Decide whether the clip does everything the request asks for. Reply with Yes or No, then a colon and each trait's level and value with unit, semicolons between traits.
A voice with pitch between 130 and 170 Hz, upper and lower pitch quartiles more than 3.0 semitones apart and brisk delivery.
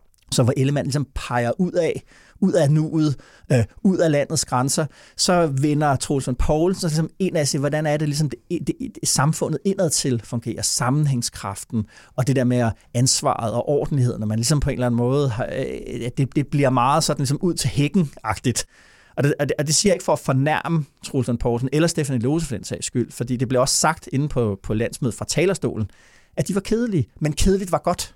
No: medium, 140 Hz; average, 4.2 semitones; average, 200 wpm